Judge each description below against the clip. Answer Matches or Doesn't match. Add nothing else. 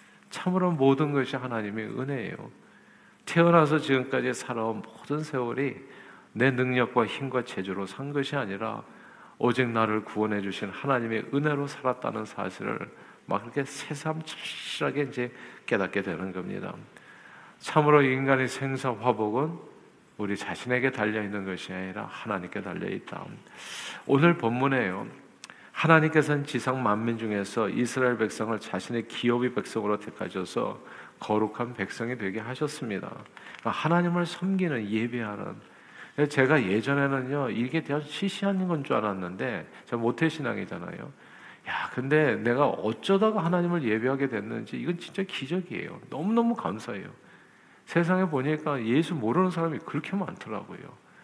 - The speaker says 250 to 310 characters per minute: Doesn't match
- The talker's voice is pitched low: Matches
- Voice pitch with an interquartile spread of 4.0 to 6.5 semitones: Matches